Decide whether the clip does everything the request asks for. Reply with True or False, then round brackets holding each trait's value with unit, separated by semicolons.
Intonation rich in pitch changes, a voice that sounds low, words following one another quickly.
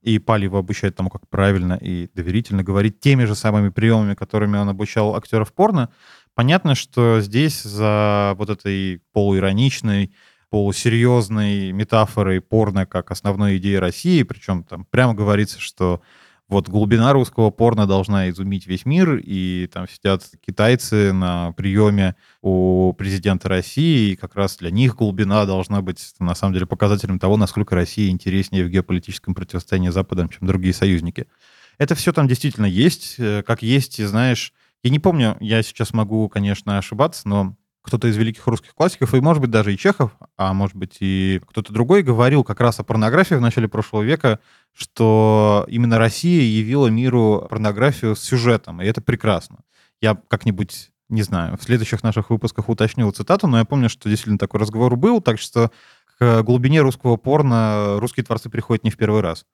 False (3.4 semitones; 105 Hz; 165 wpm)